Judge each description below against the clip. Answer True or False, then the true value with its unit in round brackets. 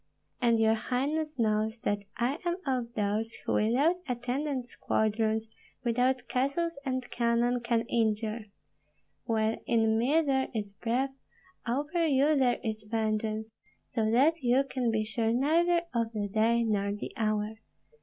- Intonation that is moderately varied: True (3.3 semitones)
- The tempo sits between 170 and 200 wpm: False (145 wpm)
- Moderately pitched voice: False (235 Hz)